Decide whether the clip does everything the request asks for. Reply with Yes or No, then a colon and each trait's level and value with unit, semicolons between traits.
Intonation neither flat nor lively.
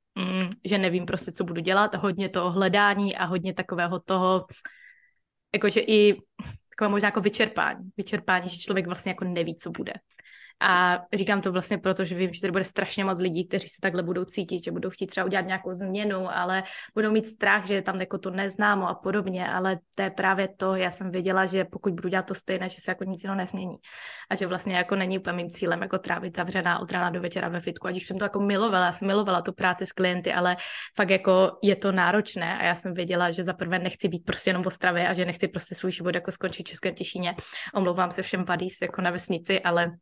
No: narrow, 1.4 semitones